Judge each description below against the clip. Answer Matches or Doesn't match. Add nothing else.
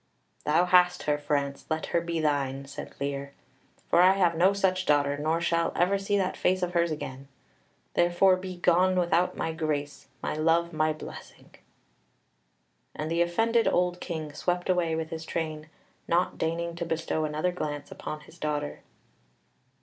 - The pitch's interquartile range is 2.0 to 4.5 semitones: Matches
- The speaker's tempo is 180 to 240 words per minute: Doesn't match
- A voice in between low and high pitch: Matches